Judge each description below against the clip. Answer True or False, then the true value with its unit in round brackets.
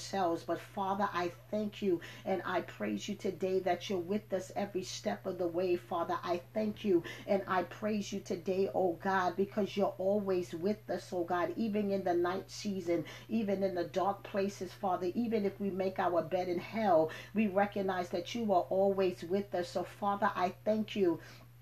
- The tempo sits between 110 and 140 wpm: False (190 wpm)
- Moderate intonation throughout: False (2.2 semitones)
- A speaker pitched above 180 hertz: True (190 Hz)